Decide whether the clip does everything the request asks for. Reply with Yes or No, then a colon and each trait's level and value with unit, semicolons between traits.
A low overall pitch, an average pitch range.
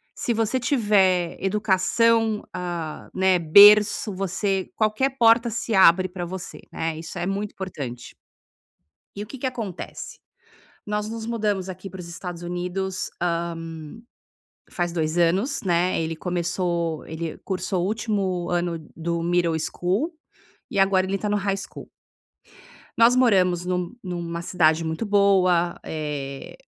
No: medium, 185 Hz; average, 3.3 semitones